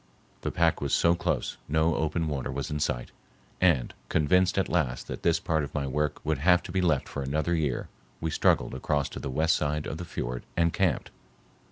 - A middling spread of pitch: Yes, average, 3.2 semitones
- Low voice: Yes, very low, 75 Hz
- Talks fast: Yes, fast, 210 wpm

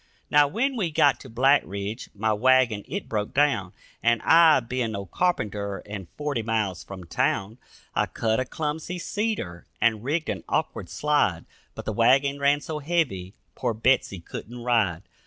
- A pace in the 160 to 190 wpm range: Yes, average, 165 wpm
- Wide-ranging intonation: Yes, wide, 6.1 semitones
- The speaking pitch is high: No, low, 120 Hz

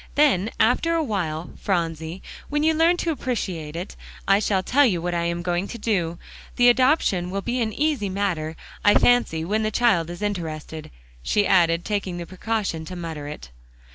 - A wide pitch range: Yes, wide, 5.7 semitones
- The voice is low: No, high, 190 Hz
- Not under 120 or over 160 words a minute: No, average, 185 wpm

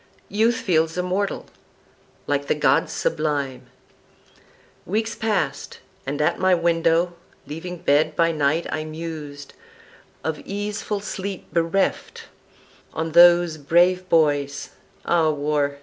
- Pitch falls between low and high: Yes, medium, 165 Hz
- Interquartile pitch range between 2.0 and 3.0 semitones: No, average, 3.4 semitones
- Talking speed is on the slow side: Yes, slow, 110 wpm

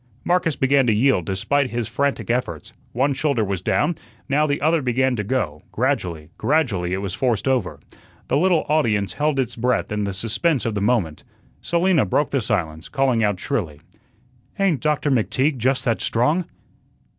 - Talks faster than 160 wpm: Yes, average, 170 wpm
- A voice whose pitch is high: No, low, 125 Hz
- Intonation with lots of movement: Yes, wide, 5.7 semitones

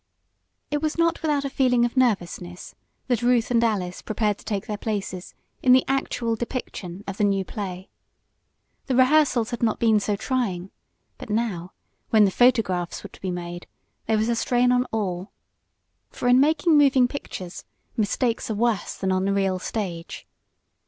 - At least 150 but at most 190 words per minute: Yes, average, 170 wpm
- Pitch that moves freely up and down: No, average, 4.6 semitones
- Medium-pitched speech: No, high, 220 Hz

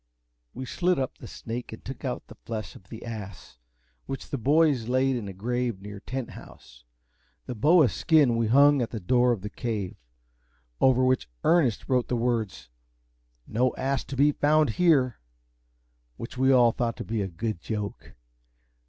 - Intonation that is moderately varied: Yes, average, 3.4 semitones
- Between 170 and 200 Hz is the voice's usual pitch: No, low, 120 Hz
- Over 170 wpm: Yes, average, 180 wpm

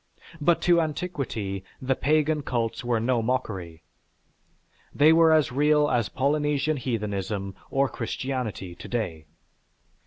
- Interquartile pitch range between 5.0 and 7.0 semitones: Yes, wide, 5.4 semitones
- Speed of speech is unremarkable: No, slow, 120 wpm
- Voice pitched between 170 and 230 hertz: No, low, 130 Hz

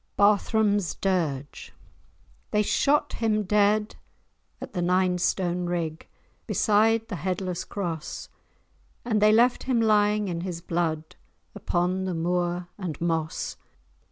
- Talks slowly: Yes, slow, 120 wpm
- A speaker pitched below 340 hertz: Yes, medium, 185 Hz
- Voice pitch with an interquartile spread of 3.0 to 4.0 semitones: Yes, average, 3.3 semitones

